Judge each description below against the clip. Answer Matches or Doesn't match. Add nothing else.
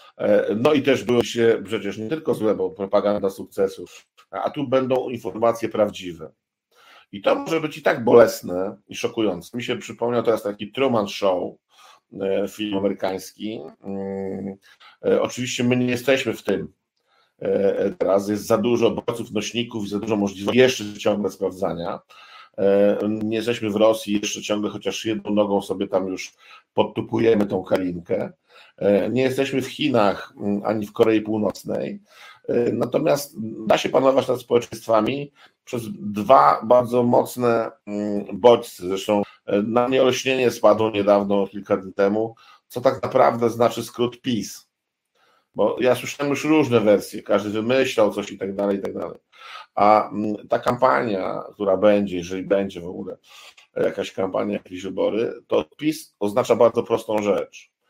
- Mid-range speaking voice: Doesn't match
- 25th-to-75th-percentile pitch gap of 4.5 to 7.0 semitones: Doesn't match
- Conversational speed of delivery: Matches